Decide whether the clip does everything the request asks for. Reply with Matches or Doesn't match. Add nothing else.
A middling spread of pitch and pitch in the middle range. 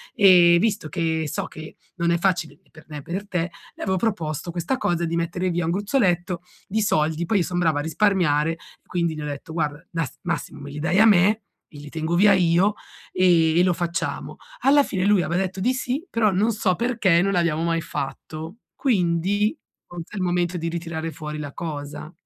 Matches